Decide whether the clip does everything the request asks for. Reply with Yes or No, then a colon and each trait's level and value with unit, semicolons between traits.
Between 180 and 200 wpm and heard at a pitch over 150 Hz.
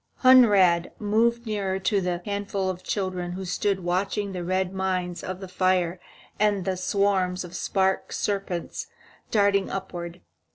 No: average, 140 wpm; high, 190 Hz